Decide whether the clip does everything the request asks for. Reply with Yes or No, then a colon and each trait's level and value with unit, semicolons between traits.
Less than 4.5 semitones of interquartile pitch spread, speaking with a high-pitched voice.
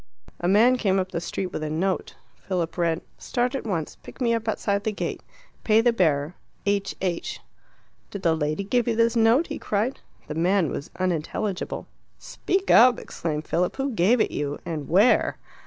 No: wide, 5.4 semitones; high, 195 Hz